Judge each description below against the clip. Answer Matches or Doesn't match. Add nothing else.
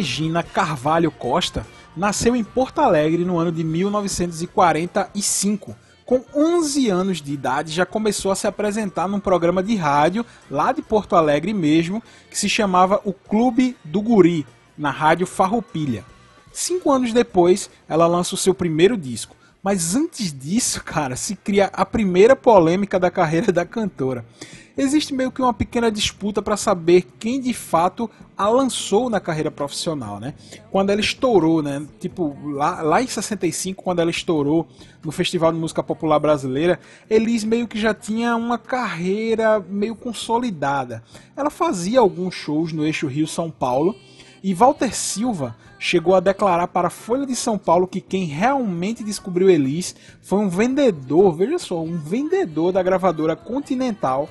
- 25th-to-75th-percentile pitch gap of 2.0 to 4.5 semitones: Doesn't match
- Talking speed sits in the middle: Matches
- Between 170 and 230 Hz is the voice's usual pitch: Matches